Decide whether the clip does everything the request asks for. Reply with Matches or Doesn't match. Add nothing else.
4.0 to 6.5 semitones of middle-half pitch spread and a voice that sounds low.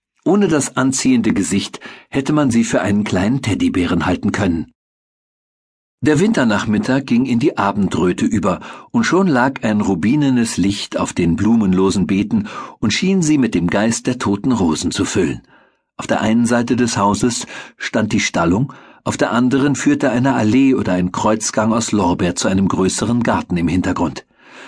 Matches